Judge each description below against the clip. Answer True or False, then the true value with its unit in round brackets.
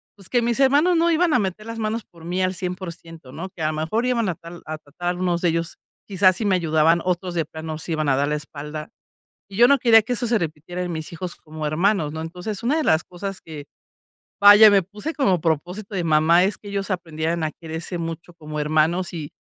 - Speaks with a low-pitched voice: False (175 Hz)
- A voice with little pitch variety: False (4.4 semitones)